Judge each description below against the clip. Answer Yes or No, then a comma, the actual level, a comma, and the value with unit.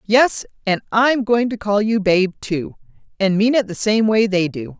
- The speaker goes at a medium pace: No, fast, 215 wpm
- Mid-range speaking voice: No, high, 205 Hz